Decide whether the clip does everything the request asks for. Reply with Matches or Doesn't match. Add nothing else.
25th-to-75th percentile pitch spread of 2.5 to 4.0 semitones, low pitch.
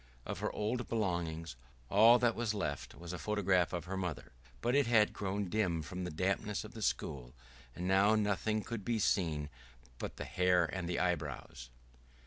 Matches